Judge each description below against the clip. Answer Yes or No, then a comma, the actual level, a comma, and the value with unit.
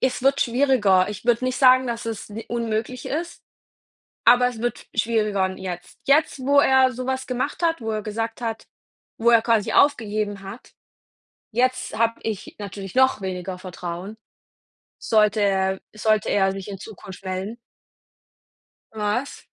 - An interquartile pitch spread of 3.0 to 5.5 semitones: Yes, average, 4.1 semitones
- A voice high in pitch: Yes, high, 225 Hz